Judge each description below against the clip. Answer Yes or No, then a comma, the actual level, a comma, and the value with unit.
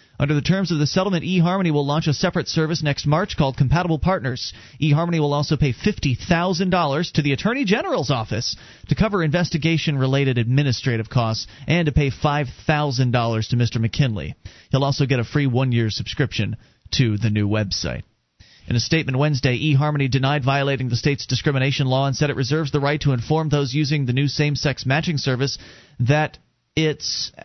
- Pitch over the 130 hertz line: Yes, medium, 140 Hz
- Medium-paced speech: Yes, average, 175 wpm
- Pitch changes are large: No, average, 3.6 semitones